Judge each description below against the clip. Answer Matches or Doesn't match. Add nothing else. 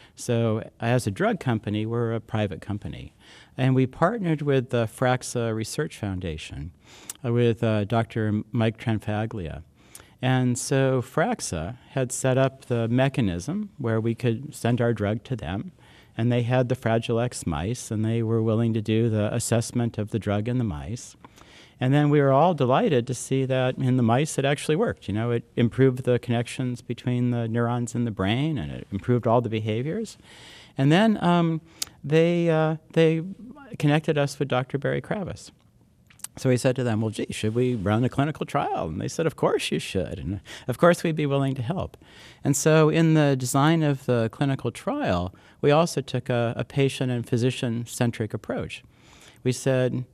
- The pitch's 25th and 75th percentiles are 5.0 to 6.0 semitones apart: Doesn't match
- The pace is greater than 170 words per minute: Matches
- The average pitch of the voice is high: Doesn't match